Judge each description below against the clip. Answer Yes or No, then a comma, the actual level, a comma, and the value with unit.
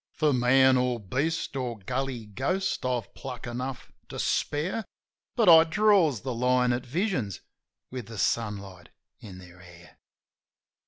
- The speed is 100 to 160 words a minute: Yes, average, 140 wpm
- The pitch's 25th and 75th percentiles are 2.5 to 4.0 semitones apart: No, average, 4.6 semitones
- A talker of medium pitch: No, low, 125 Hz